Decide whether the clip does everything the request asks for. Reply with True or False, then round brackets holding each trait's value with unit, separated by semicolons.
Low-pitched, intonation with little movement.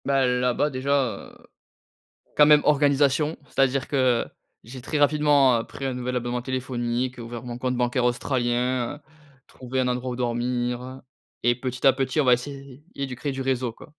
True (130 Hz; 1.9 semitones)